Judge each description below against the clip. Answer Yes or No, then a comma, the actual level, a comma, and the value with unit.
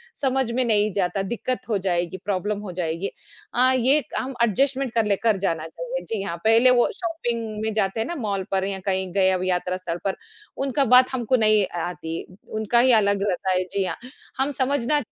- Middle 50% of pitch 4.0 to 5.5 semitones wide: Yes, average, 5.1 semitones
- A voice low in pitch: No, high, 215 Hz